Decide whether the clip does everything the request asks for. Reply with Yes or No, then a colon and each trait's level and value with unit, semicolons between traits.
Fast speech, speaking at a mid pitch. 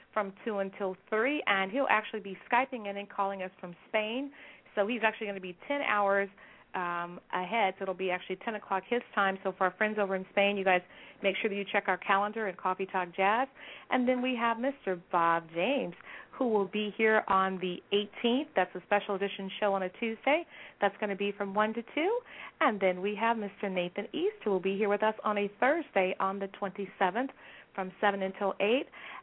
No: fast, 220 wpm; high, 205 Hz